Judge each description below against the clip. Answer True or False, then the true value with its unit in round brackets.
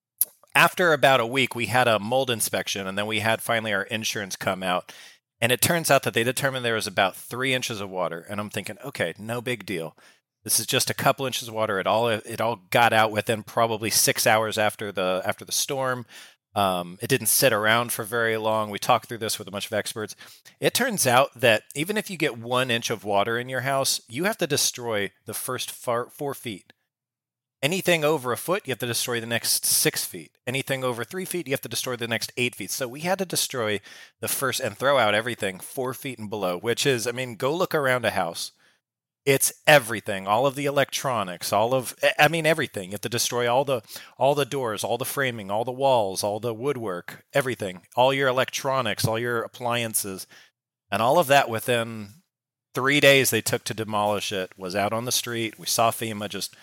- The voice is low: True (120 Hz)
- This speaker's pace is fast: True (220 wpm)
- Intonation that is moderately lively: True (3.4 semitones)